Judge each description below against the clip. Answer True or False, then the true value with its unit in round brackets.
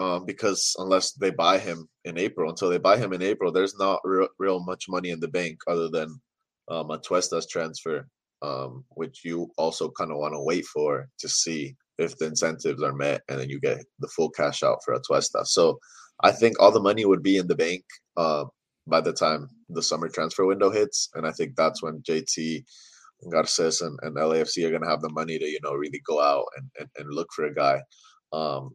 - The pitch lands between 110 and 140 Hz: False (85 Hz)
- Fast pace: True (220 wpm)